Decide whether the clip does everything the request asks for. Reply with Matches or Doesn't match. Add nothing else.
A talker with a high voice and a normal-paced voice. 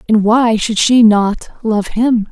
Matches